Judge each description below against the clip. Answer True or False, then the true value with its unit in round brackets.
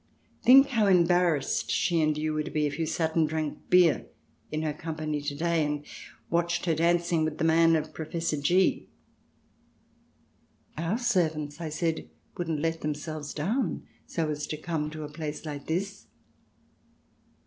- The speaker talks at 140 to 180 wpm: True (170 wpm)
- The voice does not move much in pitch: True (2.0 semitones)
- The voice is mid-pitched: True (160 Hz)